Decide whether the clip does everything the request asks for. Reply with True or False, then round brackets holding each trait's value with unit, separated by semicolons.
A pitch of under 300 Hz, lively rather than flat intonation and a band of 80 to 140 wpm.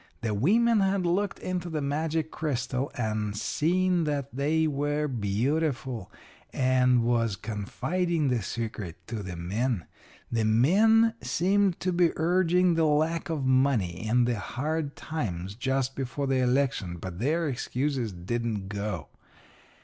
True (135 Hz; 6.4 semitones; 135 wpm)